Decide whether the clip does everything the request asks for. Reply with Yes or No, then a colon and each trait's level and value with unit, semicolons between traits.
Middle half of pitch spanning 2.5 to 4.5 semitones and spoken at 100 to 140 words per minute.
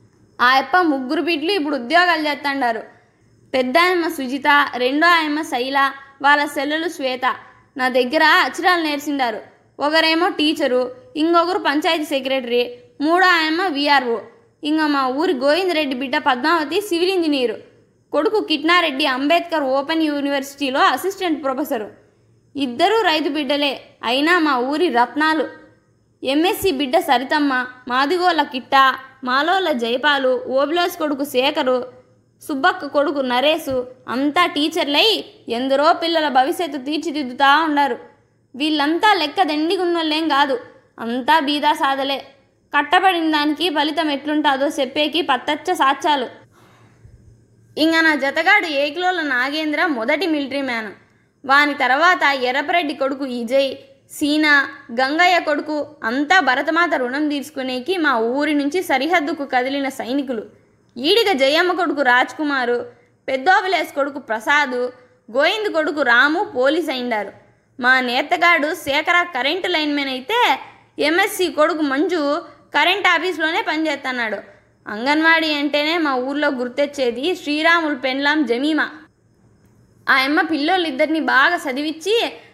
Yes: average, 3.8 semitones; average, 110 wpm